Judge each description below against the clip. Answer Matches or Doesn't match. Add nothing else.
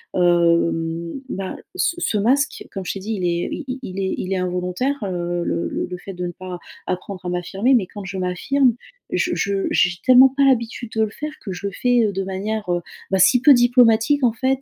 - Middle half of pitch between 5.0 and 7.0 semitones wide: Matches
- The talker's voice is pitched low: Doesn't match